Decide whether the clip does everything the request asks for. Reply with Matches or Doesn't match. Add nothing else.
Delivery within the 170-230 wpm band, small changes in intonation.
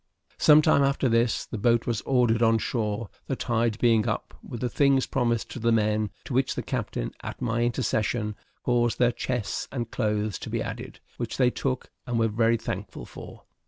Matches